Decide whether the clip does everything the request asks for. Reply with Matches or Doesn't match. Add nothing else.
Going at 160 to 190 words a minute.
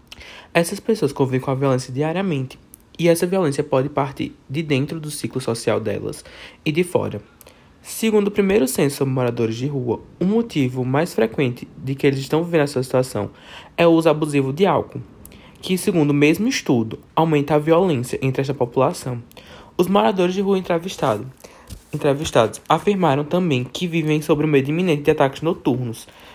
Matches